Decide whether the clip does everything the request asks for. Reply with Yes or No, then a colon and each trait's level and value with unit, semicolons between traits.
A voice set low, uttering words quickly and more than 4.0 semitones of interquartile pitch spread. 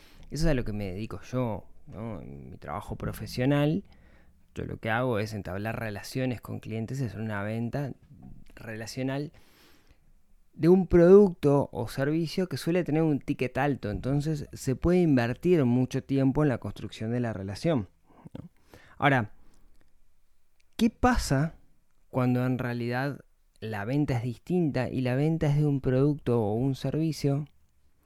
No: low, 125 Hz; average, 150 wpm; average, 5.2 semitones